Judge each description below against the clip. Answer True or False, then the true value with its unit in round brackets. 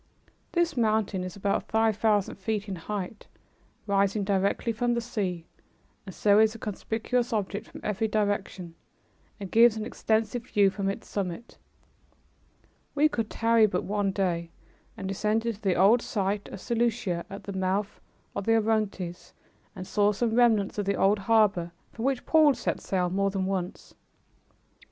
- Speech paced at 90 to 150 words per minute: False (160 wpm)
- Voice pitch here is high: True (205 Hz)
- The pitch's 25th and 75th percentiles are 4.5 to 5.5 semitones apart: False (2.6 semitones)